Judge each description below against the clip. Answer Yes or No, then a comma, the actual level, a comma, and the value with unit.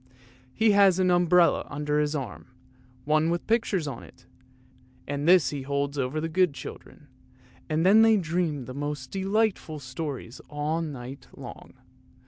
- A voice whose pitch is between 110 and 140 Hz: No, medium, 155 Hz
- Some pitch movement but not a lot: Yes, average, 4.1 semitones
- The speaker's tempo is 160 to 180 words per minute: No, average, 150 wpm